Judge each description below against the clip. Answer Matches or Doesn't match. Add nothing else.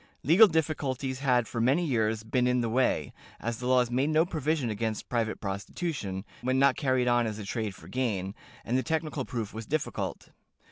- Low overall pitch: Matches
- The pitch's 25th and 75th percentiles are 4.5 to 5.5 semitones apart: Doesn't match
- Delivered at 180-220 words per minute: Matches